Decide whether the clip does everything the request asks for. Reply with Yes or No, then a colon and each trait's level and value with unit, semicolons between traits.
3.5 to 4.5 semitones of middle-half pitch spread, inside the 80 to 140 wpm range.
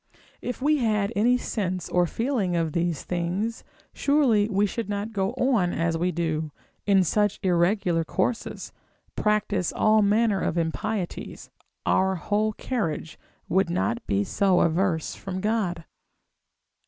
Yes: average, 4.0 semitones; slow, 135 wpm